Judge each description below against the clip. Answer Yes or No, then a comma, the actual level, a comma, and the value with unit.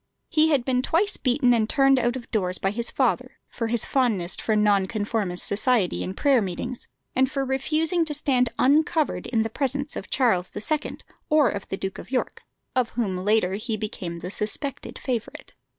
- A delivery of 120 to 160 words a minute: No, average, 180 wpm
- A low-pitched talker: No, high, 240 Hz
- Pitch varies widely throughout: No, average, 4.8 semitones